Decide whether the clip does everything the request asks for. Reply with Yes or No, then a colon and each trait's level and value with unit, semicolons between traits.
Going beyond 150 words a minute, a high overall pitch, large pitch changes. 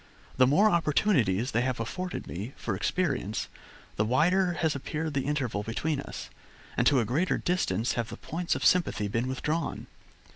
No: average, 170 wpm; medium, 140 Hz; wide, 6.6 semitones